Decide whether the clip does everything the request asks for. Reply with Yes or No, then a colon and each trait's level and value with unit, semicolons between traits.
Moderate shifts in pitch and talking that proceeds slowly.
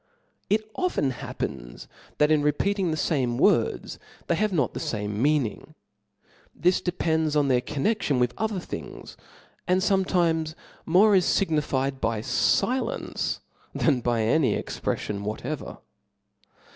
No: wide, 6.6 semitones; slow, 125 wpm